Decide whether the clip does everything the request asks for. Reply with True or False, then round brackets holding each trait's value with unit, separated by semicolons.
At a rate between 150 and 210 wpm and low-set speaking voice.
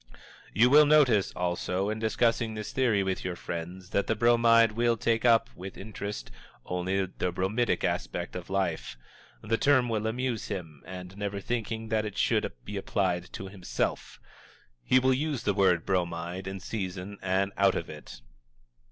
True (165 wpm; 100 Hz)